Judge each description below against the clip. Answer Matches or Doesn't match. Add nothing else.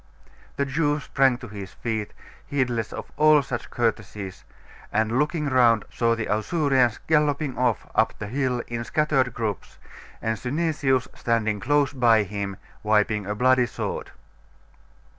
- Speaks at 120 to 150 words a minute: Matches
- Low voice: Matches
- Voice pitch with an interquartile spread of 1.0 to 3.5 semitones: Doesn't match